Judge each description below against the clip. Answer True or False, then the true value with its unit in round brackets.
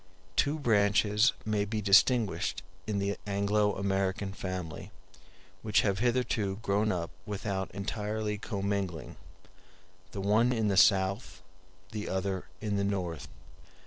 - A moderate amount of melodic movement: False (1.7 semitones)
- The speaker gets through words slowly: True (120 wpm)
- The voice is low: True (100 Hz)